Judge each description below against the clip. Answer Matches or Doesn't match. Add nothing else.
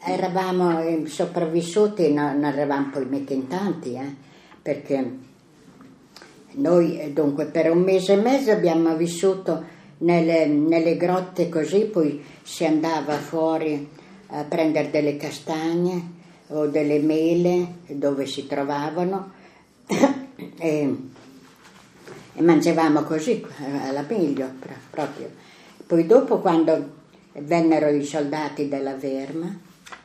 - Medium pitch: Matches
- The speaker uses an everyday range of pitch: Matches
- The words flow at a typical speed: Doesn't match